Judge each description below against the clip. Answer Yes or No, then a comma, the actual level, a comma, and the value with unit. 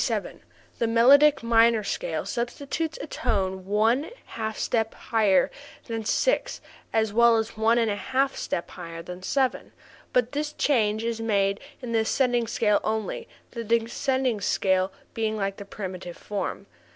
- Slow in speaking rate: No, average, 145 wpm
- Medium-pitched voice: No, high, 225 Hz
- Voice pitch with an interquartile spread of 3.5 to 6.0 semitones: No, average, 3.0 semitones